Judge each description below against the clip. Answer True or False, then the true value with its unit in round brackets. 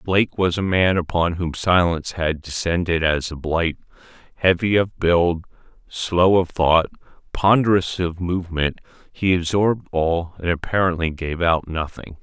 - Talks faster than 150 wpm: False (140 wpm)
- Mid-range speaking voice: False (85 Hz)